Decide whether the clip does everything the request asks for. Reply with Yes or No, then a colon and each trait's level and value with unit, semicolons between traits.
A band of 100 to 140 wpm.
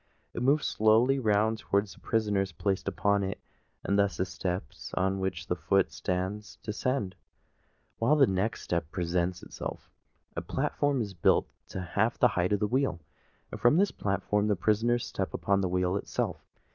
No: average, 170 wpm